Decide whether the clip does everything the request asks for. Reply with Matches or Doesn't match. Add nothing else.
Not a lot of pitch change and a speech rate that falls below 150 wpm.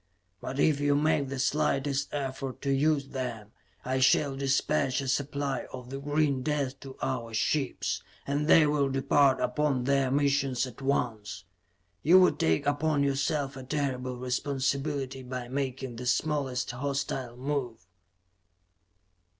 Matches